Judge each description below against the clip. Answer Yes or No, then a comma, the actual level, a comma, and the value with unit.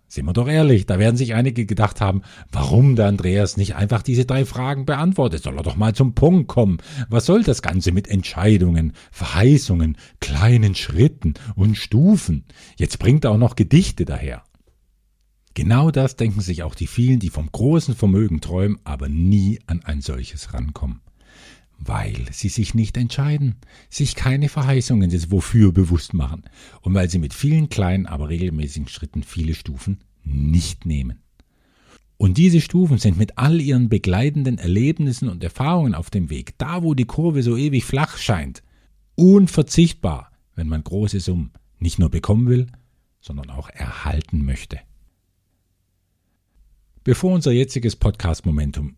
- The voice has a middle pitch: No, low, 100 Hz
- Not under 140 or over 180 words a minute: Yes, average, 155 wpm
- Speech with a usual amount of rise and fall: No, wide, 7.2 semitones